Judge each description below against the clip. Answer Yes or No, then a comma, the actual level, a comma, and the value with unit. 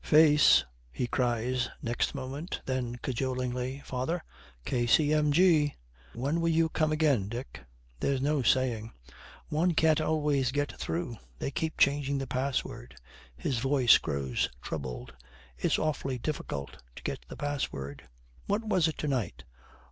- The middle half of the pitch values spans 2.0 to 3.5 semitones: No, average, 4.1 semitones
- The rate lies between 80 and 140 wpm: Yes, slow, 135 wpm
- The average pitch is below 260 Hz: Yes, low, 135 Hz